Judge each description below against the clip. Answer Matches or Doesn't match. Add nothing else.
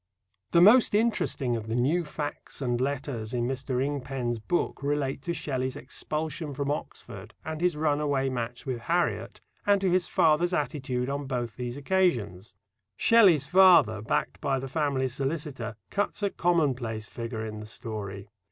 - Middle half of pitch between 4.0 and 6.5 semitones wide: Matches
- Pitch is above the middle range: Doesn't match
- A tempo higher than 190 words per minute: Doesn't match